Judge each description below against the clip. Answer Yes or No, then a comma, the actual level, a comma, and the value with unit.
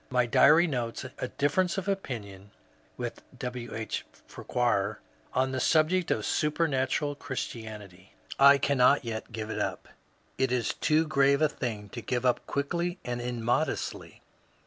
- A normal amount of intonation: Yes, average, 4.4 semitones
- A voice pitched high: No, low, 130 Hz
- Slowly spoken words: No, average, 145 wpm